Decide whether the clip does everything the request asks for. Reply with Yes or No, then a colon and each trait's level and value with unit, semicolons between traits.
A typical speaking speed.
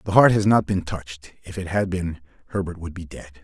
No: fast, 245 wpm